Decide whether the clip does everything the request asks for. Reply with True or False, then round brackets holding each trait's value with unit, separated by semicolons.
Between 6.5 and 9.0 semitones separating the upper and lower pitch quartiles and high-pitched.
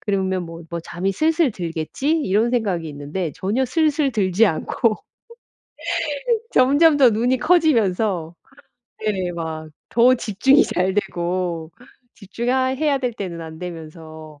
True (7.0 semitones; 195 Hz)